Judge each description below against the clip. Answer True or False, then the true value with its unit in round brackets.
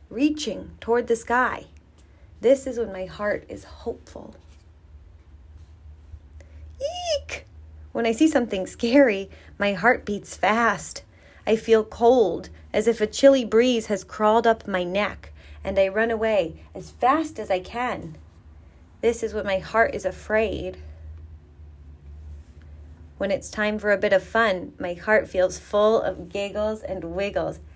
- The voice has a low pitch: False (195 Hz)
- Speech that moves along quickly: False (145 wpm)